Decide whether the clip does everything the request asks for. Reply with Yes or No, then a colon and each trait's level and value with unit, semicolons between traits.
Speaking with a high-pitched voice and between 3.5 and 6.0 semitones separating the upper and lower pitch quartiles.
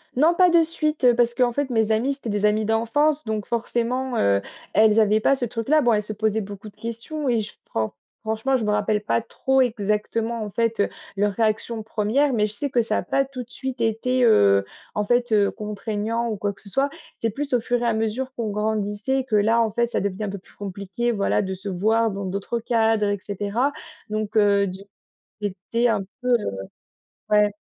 No: high, 220 Hz; average, 2.7 semitones